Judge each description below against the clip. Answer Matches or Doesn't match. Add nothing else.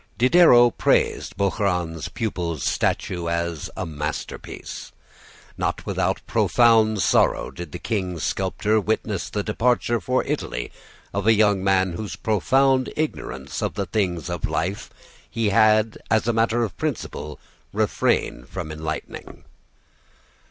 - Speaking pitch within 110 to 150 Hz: Doesn't match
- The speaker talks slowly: Matches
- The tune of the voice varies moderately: Matches